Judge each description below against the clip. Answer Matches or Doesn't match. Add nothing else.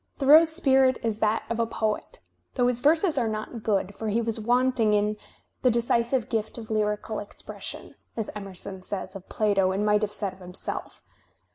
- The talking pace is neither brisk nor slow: Matches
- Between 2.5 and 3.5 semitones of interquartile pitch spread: Matches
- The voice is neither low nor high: Doesn't match